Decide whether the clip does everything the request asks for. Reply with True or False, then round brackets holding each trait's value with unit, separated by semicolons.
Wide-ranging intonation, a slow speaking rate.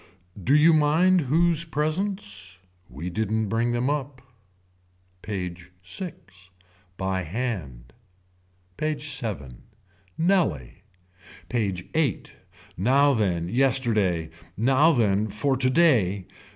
True (7.9 semitones; 95 wpm)